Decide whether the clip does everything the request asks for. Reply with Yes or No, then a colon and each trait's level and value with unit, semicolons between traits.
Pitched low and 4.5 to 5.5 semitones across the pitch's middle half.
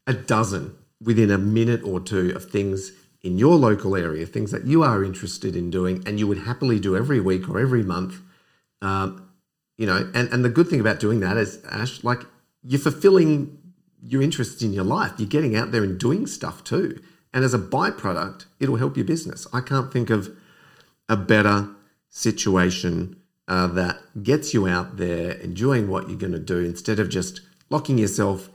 Yes: low, 110 Hz; average, 5.2 semitones